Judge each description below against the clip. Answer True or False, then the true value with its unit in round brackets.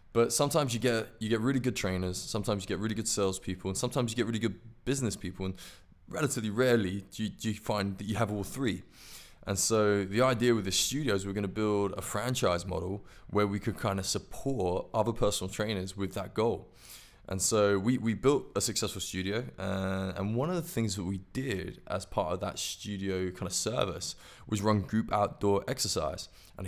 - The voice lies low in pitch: True (105 Hz)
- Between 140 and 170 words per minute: False (200 wpm)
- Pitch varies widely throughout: False (3.4 semitones)